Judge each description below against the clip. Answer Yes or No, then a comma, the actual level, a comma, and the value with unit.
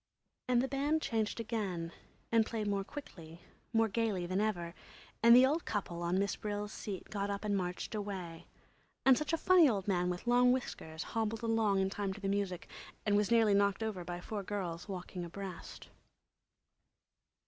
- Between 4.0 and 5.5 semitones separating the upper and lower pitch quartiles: No, average, 3.6 semitones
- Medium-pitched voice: No, high, 205 Hz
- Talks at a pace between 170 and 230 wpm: Yes, average, 180 wpm